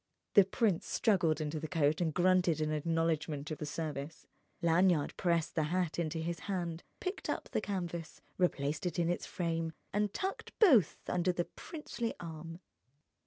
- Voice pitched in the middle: Yes, medium, 170 Hz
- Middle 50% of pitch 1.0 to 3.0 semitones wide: Yes, average, 2.7 semitones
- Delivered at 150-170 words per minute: Yes, average, 165 wpm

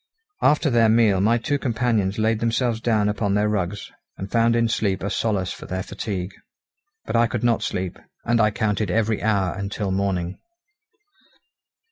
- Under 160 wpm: No, average, 165 wpm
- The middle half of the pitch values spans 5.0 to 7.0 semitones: No, average, 2.8 semitones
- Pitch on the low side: Yes, low, 105 Hz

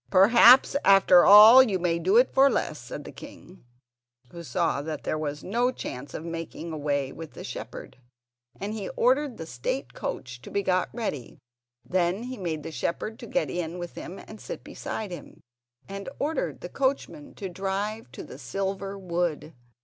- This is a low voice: No, medium, 185 Hz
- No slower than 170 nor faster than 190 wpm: Yes, average, 175 wpm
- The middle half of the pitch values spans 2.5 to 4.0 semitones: No, average, 5.0 semitones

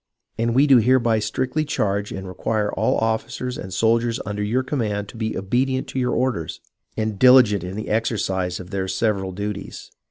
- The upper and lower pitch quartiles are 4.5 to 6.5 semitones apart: No, average, 3.7 semitones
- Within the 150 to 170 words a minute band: No, average, 185 wpm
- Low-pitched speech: Yes, low, 110 Hz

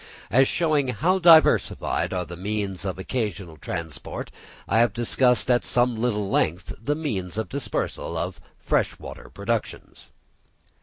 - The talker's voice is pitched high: No, low, 110 Hz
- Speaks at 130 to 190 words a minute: Yes, average, 140 wpm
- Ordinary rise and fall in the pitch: No, wide, 5.7 semitones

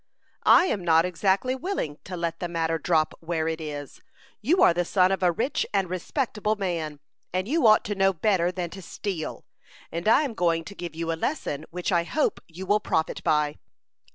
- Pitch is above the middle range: No, medium, 175 Hz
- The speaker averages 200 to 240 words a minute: Yes, fast, 205 wpm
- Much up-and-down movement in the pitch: No, average, 3.8 semitones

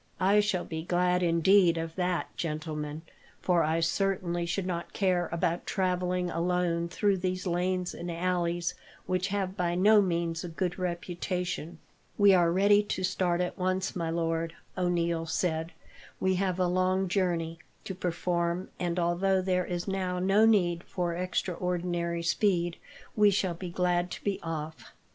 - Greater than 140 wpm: Yes, average, 155 wpm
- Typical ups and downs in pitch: No, narrow, 1.6 semitones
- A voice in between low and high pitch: Yes, medium, 180 Hz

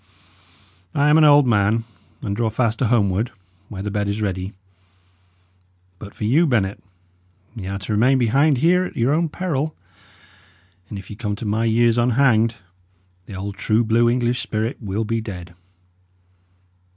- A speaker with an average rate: Yes, average, 165 wpm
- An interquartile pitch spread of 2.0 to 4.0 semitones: Yes, average, 3.6 semitones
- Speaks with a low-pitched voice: Yes, low, 115 Hz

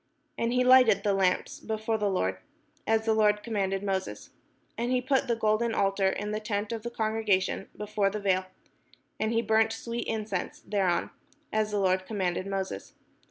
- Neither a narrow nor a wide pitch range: No, narrow, 2.3 semitones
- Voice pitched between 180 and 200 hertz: No, high, 210 Hz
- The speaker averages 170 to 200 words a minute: Yes, average, 180 wpm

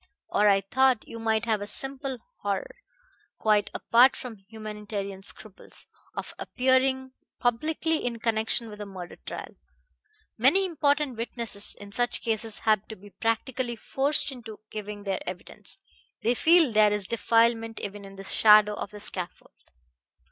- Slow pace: No, average, 150 wpm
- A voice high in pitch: Yes, high, 225 Hz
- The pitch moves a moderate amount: Yes, average, 3.5 semitones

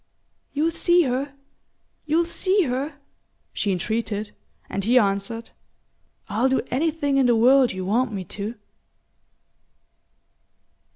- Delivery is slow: Yes, slow, 115 wpm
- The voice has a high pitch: Yes, very high, 250 Hz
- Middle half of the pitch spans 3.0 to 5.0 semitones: No, wide, 5.4 semitones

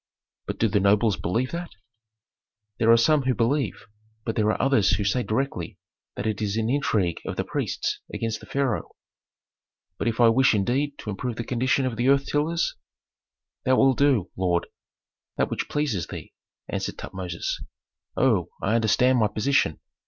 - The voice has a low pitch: Yes, low, 115 Hz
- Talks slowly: No, average, 165 wpm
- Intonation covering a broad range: No, average, 4.4 semitones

